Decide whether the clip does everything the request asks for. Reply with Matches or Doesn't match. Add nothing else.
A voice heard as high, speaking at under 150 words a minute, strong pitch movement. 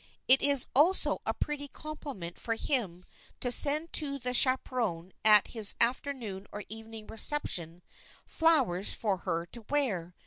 Matches